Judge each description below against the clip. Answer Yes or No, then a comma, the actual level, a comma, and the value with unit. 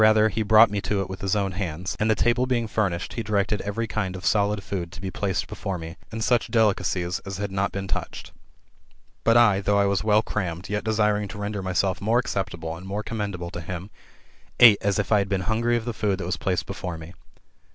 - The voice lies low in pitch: Yes, low, 100 Hz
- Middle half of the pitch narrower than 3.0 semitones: Yes, narrow, 2.5 semitones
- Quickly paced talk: Yes, fast, 245 wpm